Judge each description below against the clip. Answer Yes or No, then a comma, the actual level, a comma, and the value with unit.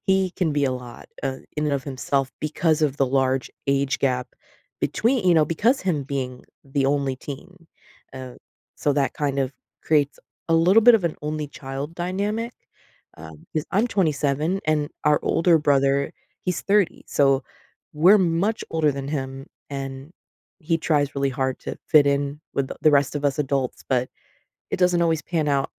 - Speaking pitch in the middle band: Yes, medium, 145 Hz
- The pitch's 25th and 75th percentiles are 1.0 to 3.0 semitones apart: No, average, 3.6 semitones